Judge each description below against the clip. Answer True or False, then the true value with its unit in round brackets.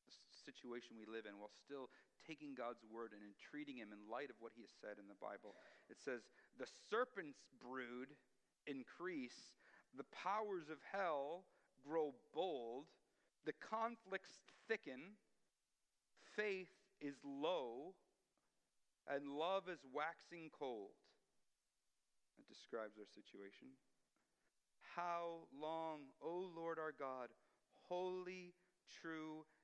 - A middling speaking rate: False (115 wpm)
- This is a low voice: False (150 Hz)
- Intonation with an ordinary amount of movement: False (6.5 semitones)